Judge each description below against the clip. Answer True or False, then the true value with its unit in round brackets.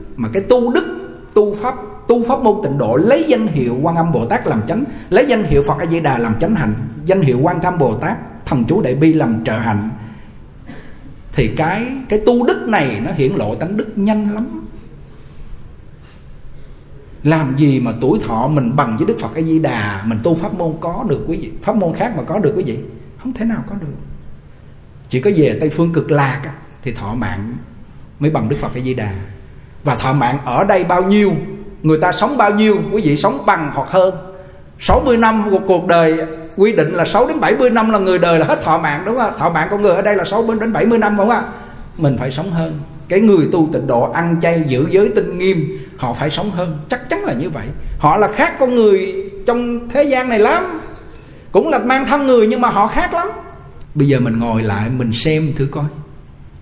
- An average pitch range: False (7.8 semitones)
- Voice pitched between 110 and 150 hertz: False (165 Hz)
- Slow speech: False (225 wpm)